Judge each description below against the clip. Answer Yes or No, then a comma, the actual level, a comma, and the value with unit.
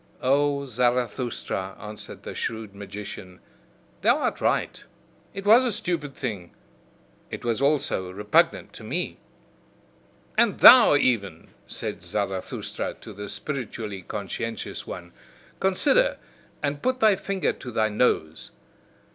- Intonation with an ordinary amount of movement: No, wide, 6.8 semitones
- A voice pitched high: No, low, 120 Hz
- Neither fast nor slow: No, slow, 120 wpm